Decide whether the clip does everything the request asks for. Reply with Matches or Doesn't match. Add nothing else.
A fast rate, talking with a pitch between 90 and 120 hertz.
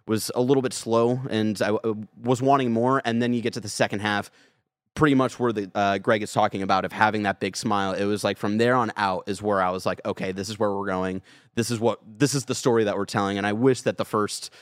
Matches